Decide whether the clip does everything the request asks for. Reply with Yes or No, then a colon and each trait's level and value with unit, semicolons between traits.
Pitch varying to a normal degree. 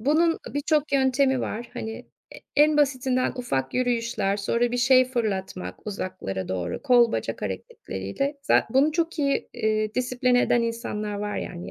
Yes: average, 4.4 semitones